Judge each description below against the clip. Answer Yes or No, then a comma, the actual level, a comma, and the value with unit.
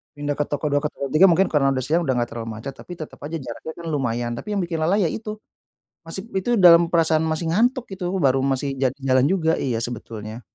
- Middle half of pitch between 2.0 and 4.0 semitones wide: No, average, 4.6 semitones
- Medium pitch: Yes, medium, 145 Hz